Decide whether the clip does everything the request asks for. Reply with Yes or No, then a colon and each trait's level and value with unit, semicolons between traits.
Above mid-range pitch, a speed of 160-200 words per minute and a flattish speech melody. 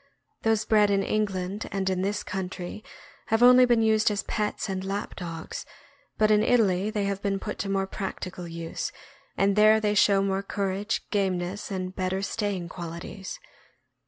Yes: high, 195 Hz; average, 170 wpm; narrow, 2.1 semitones